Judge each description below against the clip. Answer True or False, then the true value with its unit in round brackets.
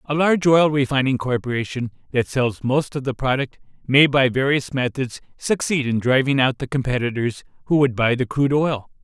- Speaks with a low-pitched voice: True (130 Hz)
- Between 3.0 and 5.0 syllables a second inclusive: False (5.3 syllables/s)